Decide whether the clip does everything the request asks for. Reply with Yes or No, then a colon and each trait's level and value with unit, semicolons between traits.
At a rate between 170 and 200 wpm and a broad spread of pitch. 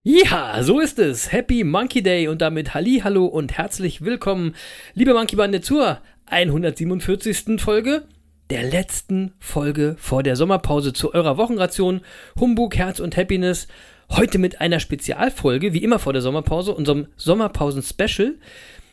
No: average, 140 wpm; wide, 5.9 semitones